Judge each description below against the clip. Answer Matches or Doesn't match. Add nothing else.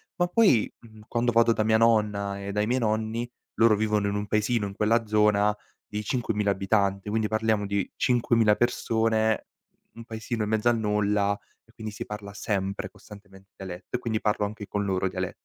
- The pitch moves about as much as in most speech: Doesn't match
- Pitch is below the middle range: Matches